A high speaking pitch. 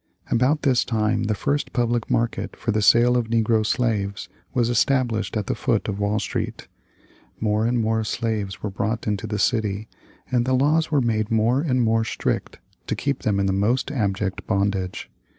No: low, 110 Hz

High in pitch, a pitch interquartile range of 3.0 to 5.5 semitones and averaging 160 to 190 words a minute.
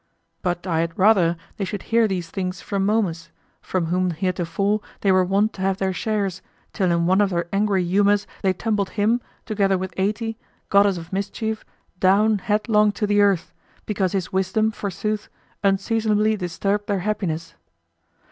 No: high, 195 Hz; narrow, 2.4 semitones; average, 165 wpm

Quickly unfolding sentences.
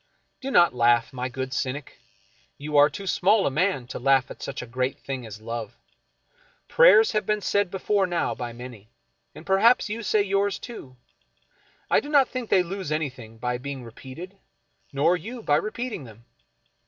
No: average, 180 wpm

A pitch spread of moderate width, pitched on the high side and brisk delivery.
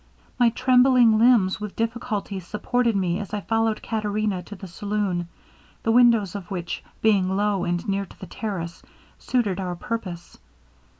No: average, 3.2 semitones; high, 205 Hz; average, 155 wpm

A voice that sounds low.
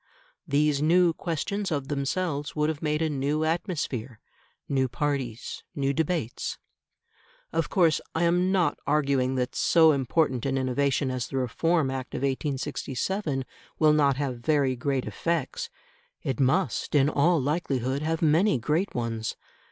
No: medium, 145 Hz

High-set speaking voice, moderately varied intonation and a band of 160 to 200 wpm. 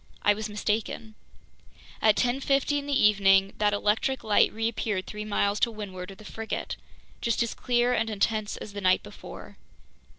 No: high, 215 Hz; narrow, 2.2 semitones; average, 165 wpm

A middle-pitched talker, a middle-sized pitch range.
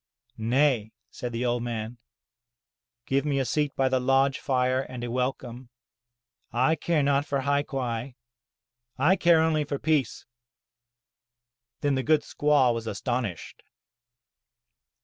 No: low, 130 Hz; average, 3.0 semitones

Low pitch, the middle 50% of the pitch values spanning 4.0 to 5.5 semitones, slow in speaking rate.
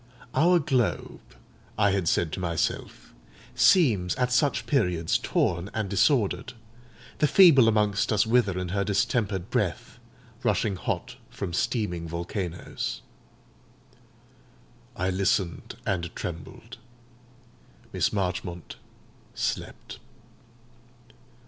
Yes: low, 100 Hz; average, 5.2 semitones; slow, 100 wpm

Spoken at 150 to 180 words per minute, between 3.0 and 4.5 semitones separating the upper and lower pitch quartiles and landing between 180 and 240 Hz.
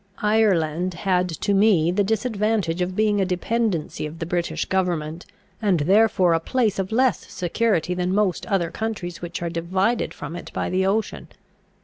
Yes: average, 165 wpm; average, 3.7 semitones; medium, 185 Hz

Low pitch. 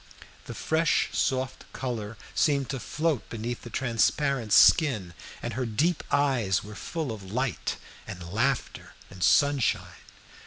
Yes: low, 125 Hz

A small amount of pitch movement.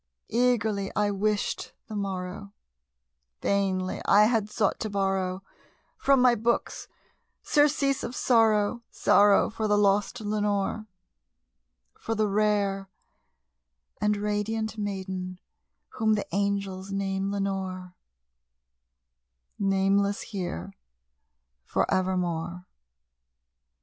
Yes: narrow, 1.8 semitones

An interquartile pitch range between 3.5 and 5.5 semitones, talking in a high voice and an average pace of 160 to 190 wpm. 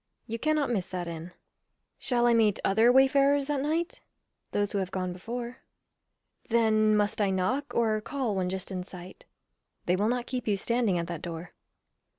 Yes: average, 4.9 semitones; high, 215 Hz; average, 175 wpm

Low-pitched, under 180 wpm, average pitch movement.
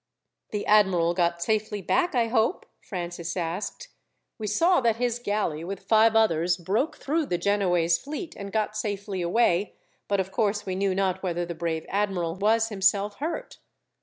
No: high, 200 Hz; average, 165 wpm; average, 4.1 semitones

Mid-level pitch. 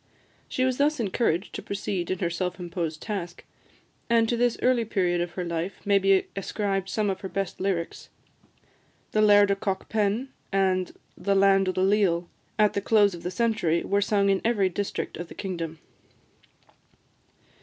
No: high, 195 Hz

